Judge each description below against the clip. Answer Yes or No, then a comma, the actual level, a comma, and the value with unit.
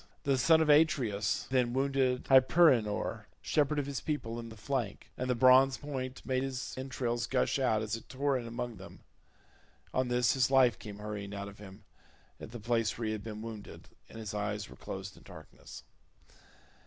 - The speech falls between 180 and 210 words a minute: Yes, average, 190 wpm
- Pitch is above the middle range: No, low, 120 Hz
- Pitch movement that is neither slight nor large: Yes, average, 3.8 semitones